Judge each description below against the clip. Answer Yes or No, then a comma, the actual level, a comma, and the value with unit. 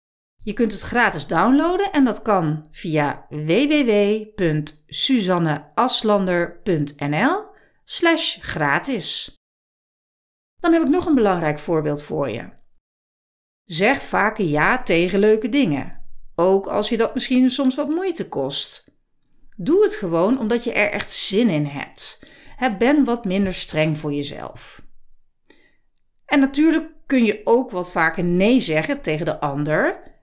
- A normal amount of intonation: No, wide, 8.4 semitones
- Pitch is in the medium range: No, high, 210 Hz